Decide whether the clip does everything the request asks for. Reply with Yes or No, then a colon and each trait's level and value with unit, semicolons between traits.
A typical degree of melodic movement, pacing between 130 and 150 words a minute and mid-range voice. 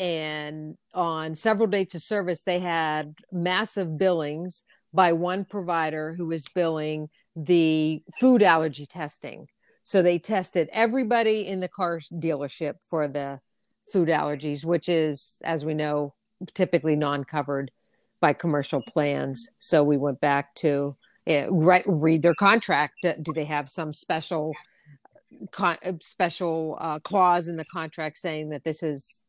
Yes: average, 3.2 semitones; slow, 135 wpm; medium, 165 Hz